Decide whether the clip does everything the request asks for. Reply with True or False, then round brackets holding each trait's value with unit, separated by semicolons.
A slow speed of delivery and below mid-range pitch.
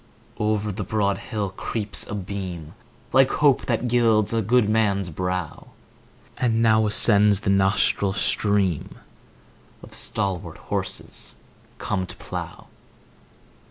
True (125 wpm; 105 Hz)